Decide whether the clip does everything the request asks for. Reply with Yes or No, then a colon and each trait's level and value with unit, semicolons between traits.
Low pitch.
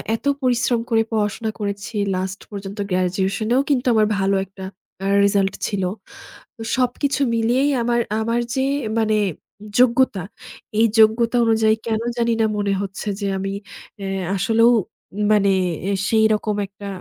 No: high, 220 Hz